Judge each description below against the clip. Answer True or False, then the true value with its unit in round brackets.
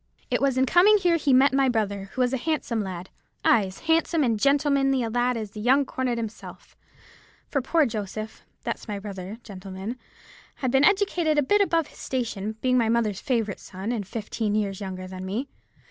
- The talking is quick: False (190 wpm)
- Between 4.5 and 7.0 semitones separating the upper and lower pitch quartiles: True (5.0 semitones)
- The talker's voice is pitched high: True (240 Hz)